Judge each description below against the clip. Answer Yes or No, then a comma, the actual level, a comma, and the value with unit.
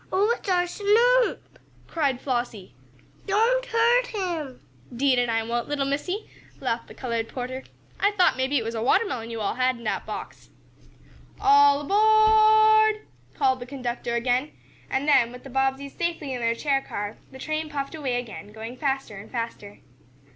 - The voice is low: No, very high, 275 Hz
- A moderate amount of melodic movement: No, wide, 7.4 semitones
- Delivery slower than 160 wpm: No, average, 170 wpm